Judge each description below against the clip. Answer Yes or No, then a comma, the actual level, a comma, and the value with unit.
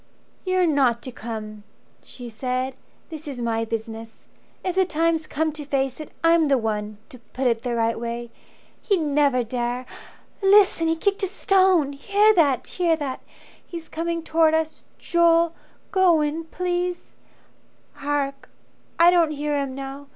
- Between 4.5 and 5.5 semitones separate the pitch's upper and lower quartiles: Yes, average, 5.1 semitones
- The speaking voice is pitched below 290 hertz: No, very high, 295 Hz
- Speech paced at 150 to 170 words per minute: Yes, average, 155 wpm